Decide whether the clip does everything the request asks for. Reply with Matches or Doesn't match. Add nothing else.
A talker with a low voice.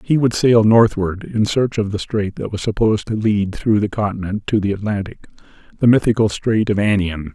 Matches